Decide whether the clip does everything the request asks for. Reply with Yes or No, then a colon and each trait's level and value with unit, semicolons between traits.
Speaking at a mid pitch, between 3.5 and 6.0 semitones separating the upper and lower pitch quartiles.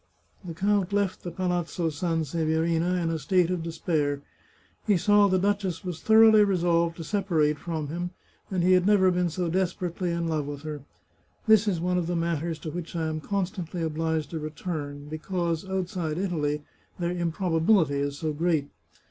No: medium, 170 Hz; narrow, 2.6 semitones